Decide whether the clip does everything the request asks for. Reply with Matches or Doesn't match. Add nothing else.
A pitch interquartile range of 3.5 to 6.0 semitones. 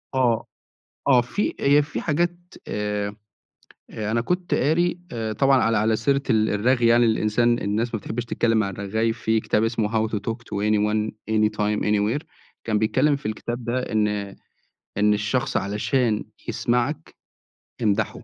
Doesn't match